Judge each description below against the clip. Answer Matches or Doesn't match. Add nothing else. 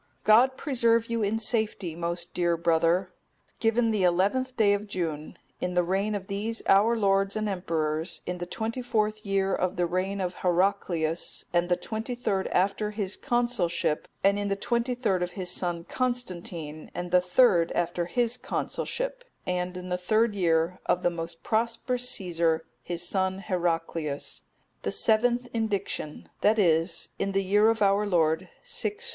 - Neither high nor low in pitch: Doesn't match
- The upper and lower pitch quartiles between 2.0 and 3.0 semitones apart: Doesn't match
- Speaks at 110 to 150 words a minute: Doesn't match